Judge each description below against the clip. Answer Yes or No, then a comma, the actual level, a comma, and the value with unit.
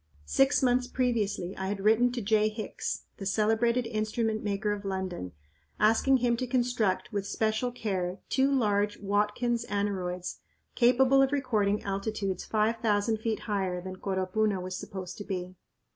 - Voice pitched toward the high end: Yes, high, 210 Hz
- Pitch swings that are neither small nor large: Yes, average, 3.3 semitones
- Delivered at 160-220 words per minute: No, average, 150 wpm